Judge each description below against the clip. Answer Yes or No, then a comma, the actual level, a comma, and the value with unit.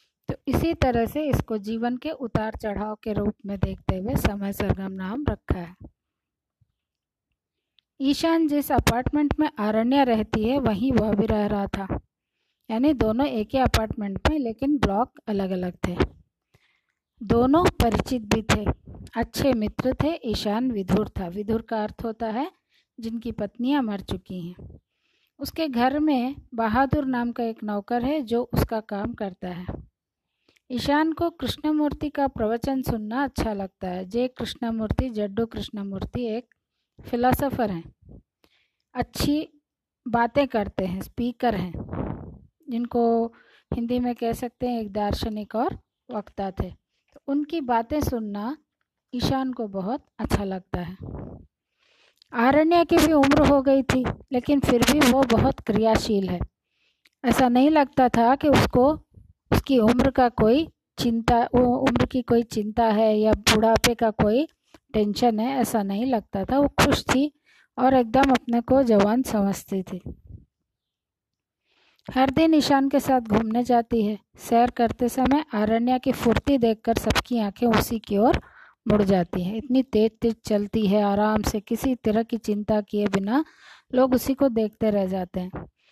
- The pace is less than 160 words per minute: Yes, average, 150 wpm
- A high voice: Yes, high, 235 Hz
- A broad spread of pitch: No, average, 3.8 semitones